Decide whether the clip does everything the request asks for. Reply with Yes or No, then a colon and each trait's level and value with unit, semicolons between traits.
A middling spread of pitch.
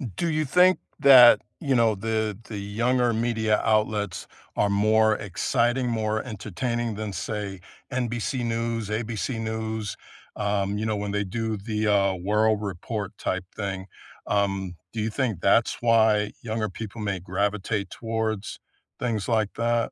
No: narrow, 2.2 semitones